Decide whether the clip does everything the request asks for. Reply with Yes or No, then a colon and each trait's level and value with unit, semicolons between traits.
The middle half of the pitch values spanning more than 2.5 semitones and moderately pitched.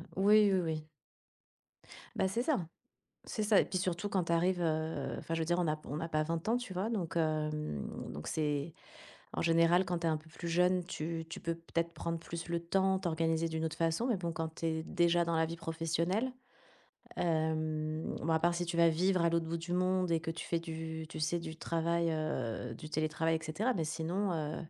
No: narrow, 1.8 semitones; medium, 165 Hz